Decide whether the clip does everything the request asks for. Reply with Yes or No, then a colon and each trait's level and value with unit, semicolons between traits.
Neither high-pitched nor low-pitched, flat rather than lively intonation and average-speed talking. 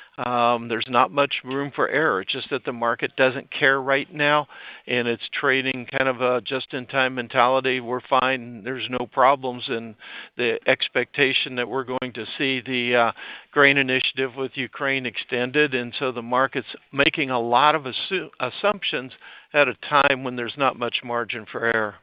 No: low, 130 Hz; narrow, 2.0 semitones; average, 175 wpm